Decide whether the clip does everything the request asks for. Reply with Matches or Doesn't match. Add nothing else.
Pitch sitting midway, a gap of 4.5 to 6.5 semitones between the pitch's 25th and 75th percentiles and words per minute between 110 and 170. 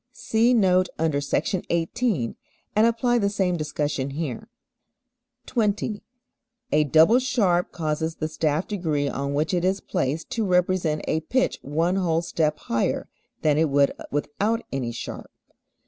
Matches